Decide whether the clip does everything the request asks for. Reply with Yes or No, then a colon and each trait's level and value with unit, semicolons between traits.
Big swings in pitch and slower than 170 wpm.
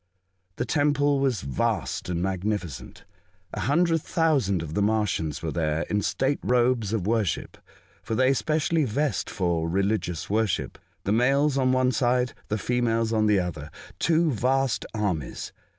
Yes: wide, 6.3 semitones; average, 150 wpm